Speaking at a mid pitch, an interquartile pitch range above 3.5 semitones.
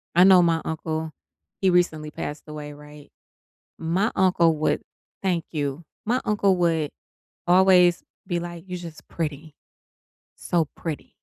No: medium, 170 Hz; narrow, 2.5 semitones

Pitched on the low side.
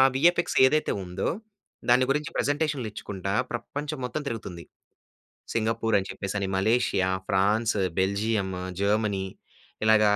Yes: low, 110 Hz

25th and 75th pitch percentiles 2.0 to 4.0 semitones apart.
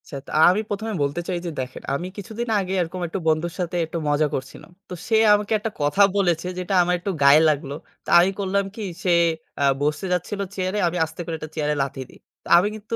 No: average, 4.5 semitones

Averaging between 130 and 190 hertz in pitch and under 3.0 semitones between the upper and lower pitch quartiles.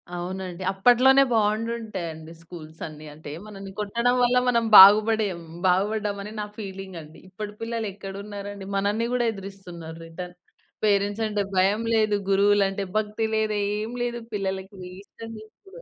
No: high, 205 Hz; narrow, 2.4 semitones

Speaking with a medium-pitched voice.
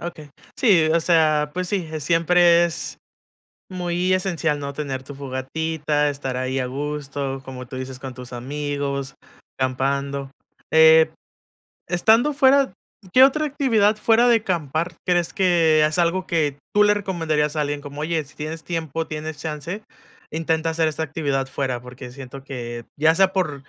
Yes: medium, 155 Hz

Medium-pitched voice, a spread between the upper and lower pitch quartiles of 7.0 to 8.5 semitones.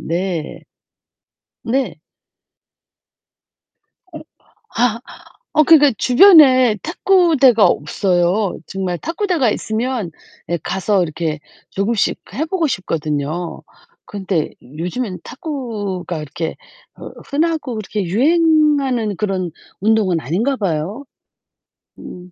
No: high, 210 Hz; wide, 7.5 semitones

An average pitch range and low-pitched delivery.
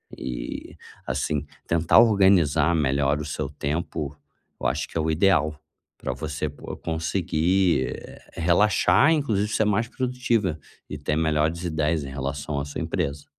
Yes: average, 4.7 semitones; very low, 80 Hz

